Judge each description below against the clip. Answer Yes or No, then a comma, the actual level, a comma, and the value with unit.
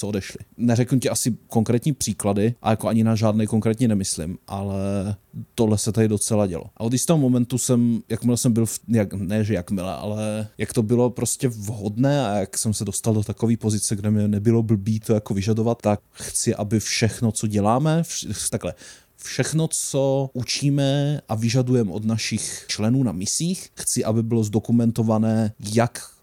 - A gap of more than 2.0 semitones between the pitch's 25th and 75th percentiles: Yes, narrow, 2.4 semitones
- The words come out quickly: Yes, fast, 175 wpm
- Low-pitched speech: Yes, low, 110 Hz